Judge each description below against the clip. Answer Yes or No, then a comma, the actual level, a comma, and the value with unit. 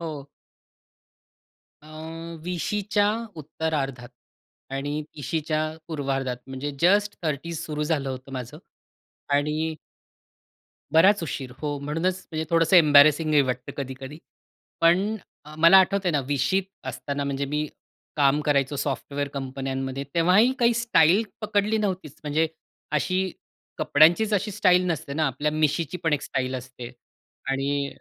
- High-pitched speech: No, medium, 150 Hz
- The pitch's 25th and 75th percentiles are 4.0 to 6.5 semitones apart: No, average, 3.4 semitones